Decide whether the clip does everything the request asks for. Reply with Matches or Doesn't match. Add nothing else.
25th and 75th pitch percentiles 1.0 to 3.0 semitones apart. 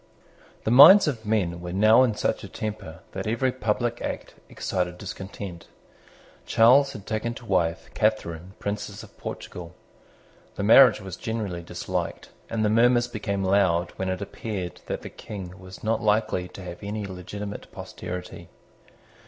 Doesn't match